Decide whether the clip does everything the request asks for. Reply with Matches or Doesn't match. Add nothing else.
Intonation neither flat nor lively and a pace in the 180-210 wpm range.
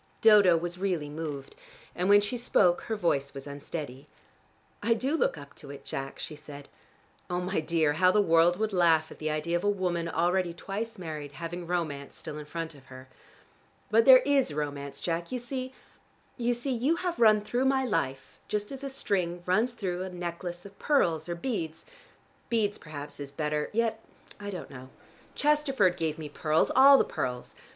Doesn't match